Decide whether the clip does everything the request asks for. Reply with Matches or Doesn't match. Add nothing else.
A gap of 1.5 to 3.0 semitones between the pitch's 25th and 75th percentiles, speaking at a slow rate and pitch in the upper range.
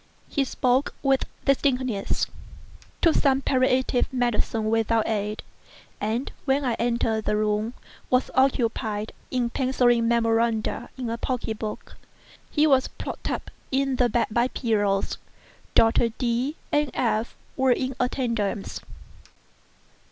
Matches